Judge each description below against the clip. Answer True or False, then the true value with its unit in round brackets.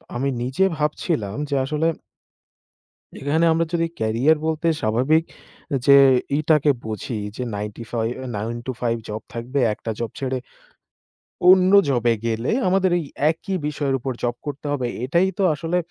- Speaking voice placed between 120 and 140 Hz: True (135 Hz)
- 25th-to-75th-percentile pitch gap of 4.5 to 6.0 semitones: True (5.2 semitones)